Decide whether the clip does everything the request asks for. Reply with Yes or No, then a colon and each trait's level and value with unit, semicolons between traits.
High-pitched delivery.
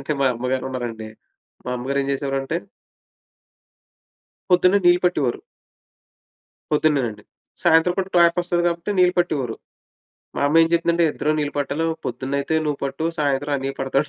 No: medium, 145 Hz